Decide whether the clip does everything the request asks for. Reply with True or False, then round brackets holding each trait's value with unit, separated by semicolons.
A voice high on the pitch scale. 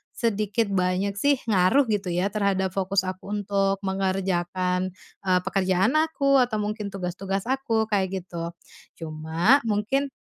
True (195 Hz)